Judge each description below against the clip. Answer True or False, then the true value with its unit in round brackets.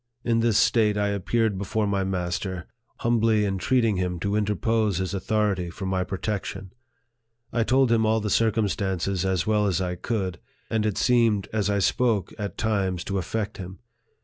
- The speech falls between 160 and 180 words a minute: True (175 wpm)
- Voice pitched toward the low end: True (105 Hz)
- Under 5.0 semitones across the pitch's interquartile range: True (2.8 semitones)